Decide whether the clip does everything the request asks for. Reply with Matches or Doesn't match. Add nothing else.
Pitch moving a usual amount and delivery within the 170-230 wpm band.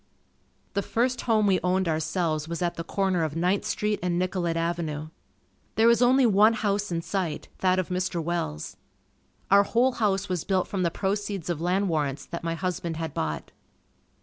Matches